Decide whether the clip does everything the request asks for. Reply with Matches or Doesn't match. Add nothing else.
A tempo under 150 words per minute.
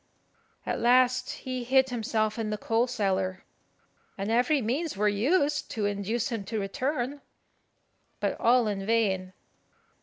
Matches